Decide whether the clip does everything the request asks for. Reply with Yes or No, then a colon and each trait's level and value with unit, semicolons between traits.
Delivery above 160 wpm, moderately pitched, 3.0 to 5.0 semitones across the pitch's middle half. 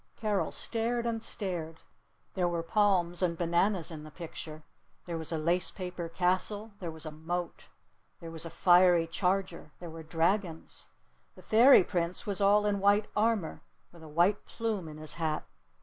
Yes: average, 170 wpm; medium, 175 Hz; average, 3.7 semitones